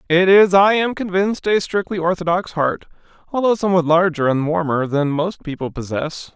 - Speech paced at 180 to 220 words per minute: No, average, 170 wpm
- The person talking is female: No, male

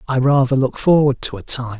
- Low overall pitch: Yes, low, 130 Hz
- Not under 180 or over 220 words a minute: No, fast, 235 wpm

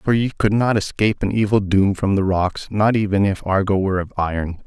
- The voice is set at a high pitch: No, low, 100 Hz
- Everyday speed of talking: No, fast, 230 wpm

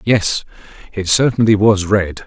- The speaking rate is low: Yes, slow, 130 wpm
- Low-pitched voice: Yes, low, 100 Hz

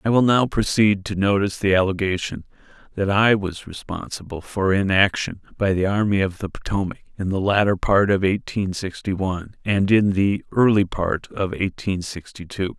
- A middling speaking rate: Yes, average, 175 wpm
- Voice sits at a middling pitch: No, low, 100 Hz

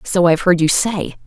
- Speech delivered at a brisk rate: Yes, fast, 285 wpm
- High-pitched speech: No, medium, 180 Hz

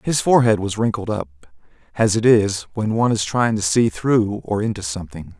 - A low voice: Yes, low, 105 Hz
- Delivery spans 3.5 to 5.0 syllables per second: No, 5.2 syllables/s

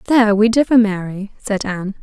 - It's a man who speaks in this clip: No, female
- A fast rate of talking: No, average, 180 wpm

